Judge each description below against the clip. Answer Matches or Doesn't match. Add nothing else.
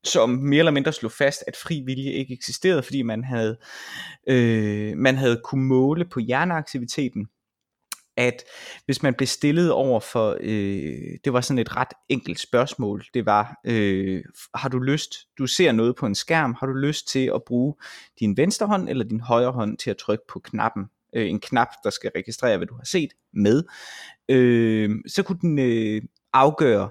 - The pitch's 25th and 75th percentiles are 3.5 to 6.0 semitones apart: Matches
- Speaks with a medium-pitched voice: Doesn't match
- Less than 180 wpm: Doesn't match